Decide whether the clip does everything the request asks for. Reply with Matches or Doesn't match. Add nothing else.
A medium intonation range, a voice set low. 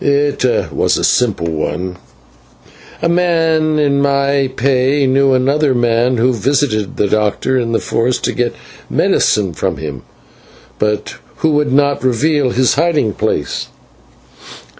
Matches